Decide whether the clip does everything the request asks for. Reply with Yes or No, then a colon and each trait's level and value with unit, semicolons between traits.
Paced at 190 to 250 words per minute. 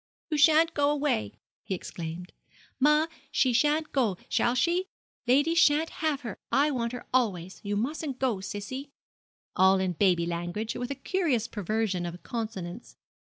No: average, 155 wpm